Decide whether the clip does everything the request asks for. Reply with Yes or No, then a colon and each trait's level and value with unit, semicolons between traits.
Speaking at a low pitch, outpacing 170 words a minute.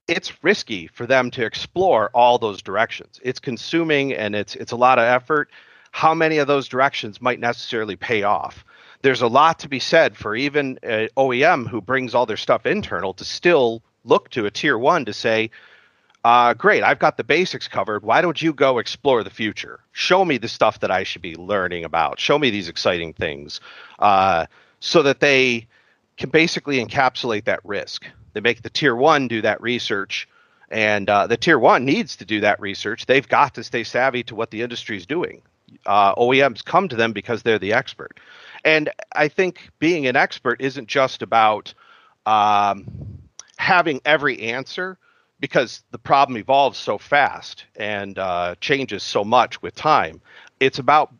Yes: low, 125 Hz; average, 185 wpm